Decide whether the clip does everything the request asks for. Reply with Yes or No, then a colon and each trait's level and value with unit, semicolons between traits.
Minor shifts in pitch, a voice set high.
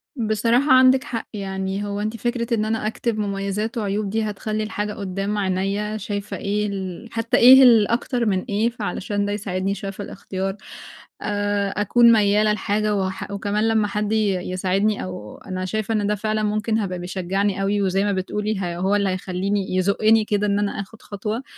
Yes: narrow, 1.8 semitones; high, 205 Hz